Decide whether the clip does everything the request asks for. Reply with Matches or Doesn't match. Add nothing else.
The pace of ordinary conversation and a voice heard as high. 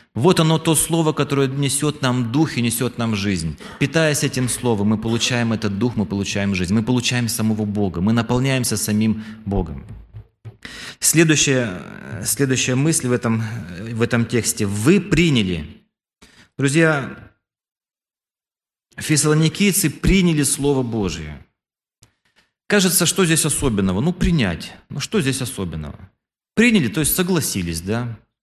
Doesn't match